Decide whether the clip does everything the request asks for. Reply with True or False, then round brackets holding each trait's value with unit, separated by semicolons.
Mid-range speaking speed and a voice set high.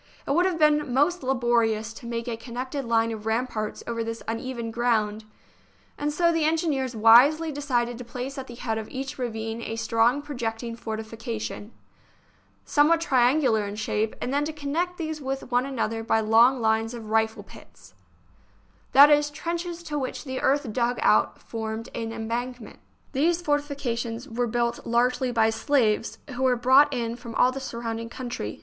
True (175 wpm; 245 Hz)